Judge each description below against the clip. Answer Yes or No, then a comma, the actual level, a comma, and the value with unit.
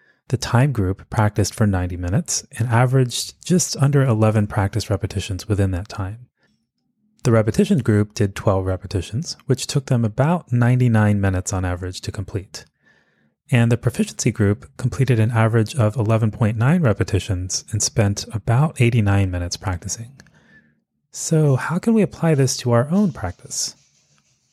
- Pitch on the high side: No, low, 115 Hz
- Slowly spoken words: No, average, 145 wpm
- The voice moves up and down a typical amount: Yes, average, 4.5 semitones